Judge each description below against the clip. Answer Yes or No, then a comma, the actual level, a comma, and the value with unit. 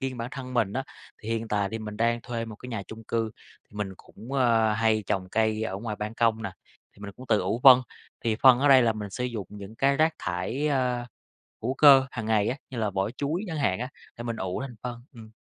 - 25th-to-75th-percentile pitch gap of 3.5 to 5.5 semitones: No, average, 3.1 semitones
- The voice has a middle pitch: No, low, 115 Hz